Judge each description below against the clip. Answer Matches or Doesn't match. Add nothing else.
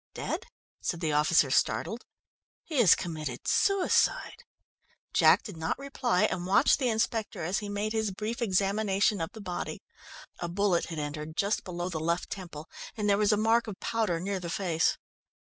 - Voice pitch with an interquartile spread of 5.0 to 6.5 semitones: Doesn't match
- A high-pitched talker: Matches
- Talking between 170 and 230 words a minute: Matches